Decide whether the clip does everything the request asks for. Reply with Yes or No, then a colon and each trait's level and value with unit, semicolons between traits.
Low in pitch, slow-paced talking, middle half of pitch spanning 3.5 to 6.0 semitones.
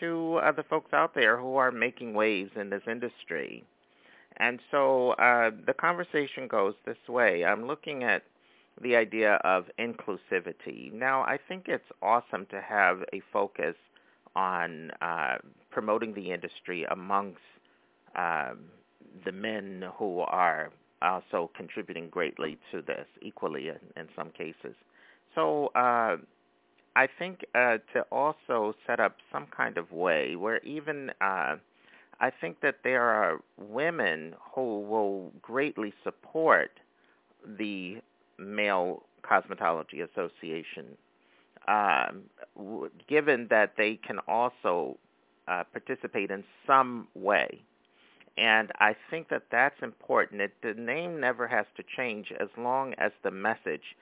Yes: low, 110 Hz; slow, 130 wpm; average, 5.1 semitones